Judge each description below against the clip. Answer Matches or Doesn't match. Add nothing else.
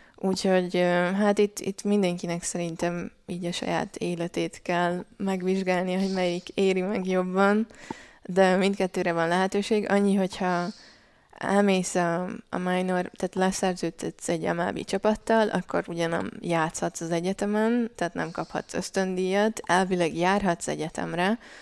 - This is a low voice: Doesn't match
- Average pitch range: Doesn't match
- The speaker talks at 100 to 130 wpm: Matches